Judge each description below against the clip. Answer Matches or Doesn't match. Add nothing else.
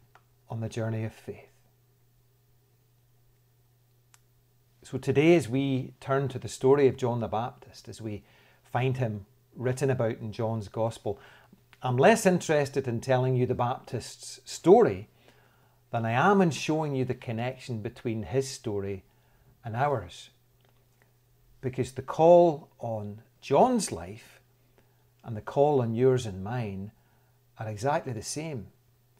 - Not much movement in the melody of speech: Matches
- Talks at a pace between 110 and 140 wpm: Matches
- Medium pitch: Doesn't match